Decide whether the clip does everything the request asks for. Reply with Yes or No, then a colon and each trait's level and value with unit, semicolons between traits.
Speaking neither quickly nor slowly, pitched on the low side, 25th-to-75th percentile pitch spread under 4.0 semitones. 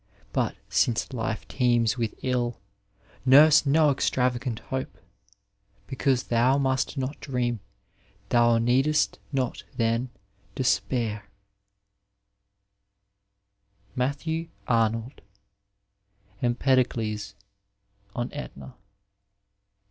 No: slow, 75 wpm; low, 125 Hz; narrow, 2.5 semitones